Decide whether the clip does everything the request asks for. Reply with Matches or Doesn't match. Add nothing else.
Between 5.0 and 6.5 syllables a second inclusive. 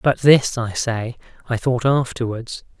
Doesn't match